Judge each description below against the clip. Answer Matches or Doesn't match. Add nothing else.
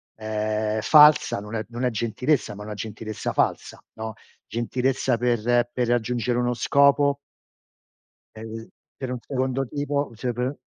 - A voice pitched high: Doesn't match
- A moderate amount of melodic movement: Matches